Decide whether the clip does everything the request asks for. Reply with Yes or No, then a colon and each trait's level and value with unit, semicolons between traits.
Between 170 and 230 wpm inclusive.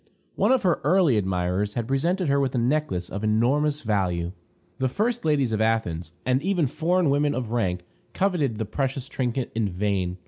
Yes: average, 180 wpm